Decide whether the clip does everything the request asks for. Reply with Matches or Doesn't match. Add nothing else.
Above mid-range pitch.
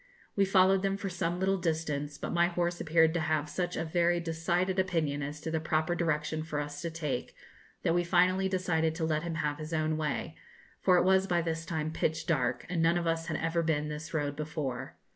Doesn't match